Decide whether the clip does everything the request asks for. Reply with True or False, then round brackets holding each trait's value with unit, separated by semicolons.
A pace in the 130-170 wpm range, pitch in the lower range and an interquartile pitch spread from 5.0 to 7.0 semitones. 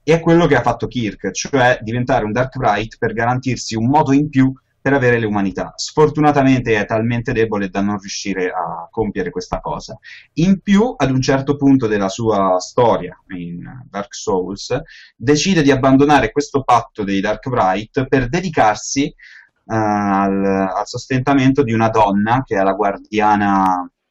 True (160 wpm; 120 Hz; 5.6 semitones)